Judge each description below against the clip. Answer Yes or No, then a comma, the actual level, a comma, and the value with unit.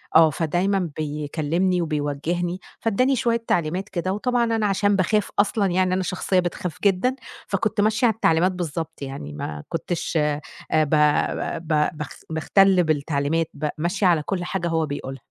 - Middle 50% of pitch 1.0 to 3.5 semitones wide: No, average, 4.1 semitones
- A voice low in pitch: No, medium, 175 Hz